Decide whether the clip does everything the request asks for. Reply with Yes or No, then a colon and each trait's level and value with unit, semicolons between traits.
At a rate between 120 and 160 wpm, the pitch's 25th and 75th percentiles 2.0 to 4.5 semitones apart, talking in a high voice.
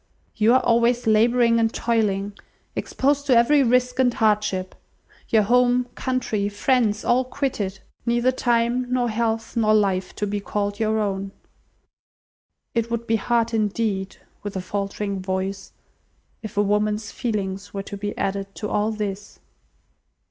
Yes: average, 140 wpm; average, 2.9 semitones; high, 220 Hz